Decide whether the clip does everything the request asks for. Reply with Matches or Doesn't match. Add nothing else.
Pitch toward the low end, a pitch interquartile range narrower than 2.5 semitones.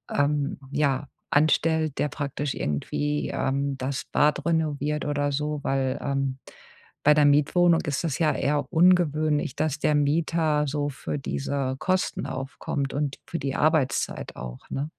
Doesn't match